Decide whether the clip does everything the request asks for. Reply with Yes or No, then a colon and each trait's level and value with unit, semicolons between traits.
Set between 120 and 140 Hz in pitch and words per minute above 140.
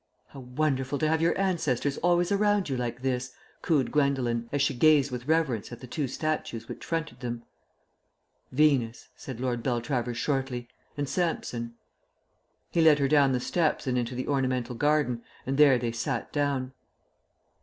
Yes: low, 135 Hz; average, 165 wpm